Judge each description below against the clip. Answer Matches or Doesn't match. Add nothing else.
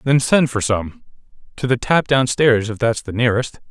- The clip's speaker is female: Doesn't match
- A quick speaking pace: Doesn't match